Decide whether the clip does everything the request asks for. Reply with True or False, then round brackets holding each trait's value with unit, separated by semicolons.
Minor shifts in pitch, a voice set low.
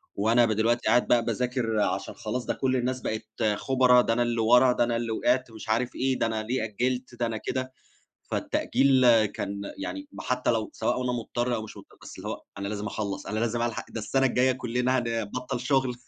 True (2.3 semitones; 120 Hz)